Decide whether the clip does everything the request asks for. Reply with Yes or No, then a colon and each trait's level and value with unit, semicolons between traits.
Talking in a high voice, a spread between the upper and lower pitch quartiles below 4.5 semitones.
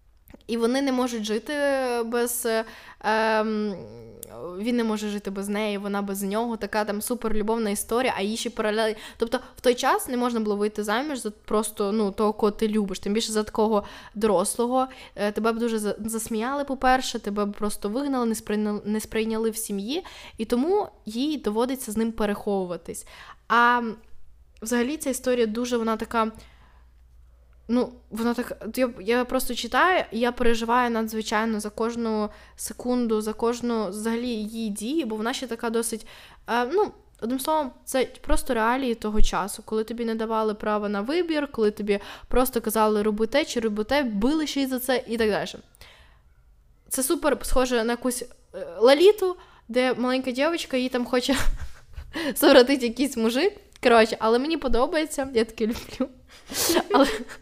Yes: high, 230 Hz; average, 3.1 semitones